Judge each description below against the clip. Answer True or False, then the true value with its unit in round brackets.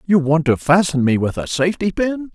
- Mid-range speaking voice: True (165 Hz)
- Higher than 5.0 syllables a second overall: True (5.5 syllables/s)